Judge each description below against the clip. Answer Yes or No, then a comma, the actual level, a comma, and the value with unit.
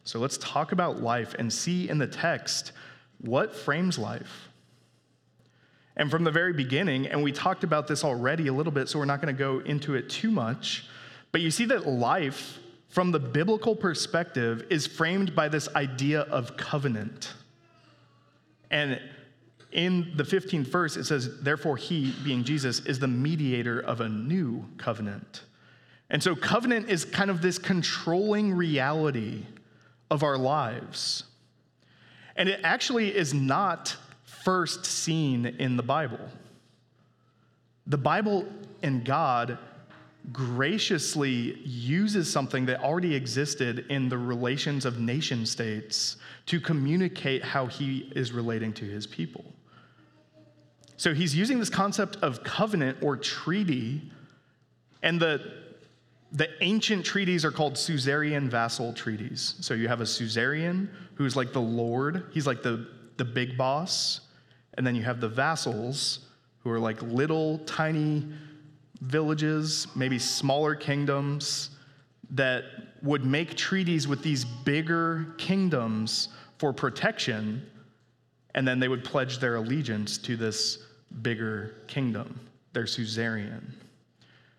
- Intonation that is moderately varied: Yes, average, 4.8 semitones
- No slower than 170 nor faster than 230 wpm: No, slow, 135 wpm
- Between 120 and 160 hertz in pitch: Yes, medium, 140 Hz